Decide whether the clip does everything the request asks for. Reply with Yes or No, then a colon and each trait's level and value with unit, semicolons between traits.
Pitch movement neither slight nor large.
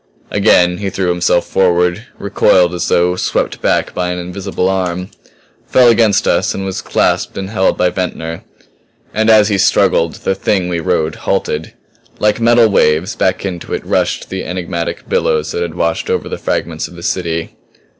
No: narrow, 2.1 semitones